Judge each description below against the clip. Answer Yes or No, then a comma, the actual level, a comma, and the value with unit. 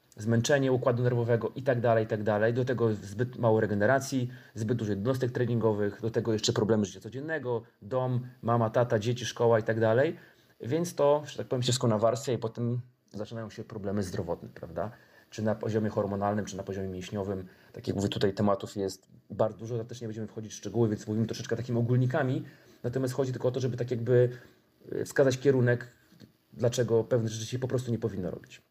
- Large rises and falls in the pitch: No, narrow, 2.5 semitones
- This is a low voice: Yes, low, 115 Hz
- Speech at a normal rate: No, fast, 190 wpm